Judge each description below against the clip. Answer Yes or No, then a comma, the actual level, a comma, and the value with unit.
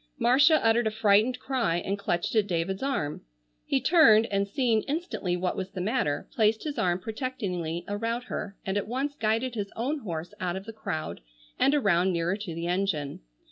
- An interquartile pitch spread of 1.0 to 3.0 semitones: No, average, 5.1 semitones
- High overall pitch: Yes, high, 205 Hz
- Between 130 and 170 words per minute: No, average, 185 wpm